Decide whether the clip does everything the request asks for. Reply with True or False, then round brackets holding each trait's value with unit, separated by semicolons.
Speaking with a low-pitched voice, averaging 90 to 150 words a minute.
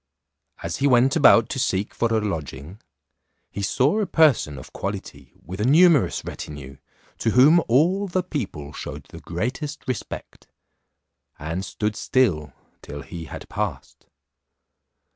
True (115 Hz; 140 wpm)